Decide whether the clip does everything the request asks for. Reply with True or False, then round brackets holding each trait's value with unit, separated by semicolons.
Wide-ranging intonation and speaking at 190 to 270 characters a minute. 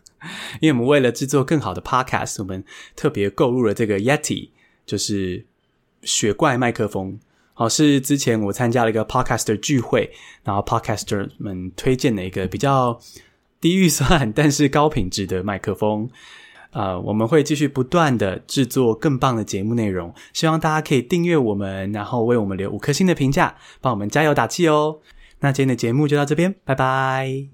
False (5.7 semitones; 330 characters per minute)